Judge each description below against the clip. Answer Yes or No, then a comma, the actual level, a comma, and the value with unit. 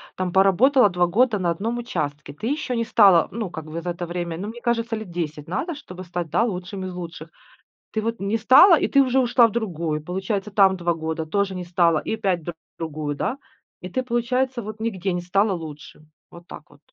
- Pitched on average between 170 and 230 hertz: Yes, high, 190 Hz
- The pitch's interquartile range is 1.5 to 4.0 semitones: No, average, 5.1 semitones